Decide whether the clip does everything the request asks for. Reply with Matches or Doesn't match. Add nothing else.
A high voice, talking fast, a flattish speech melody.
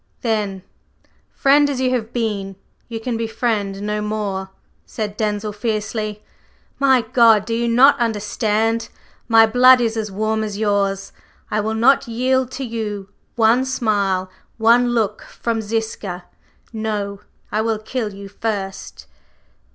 Doesn't match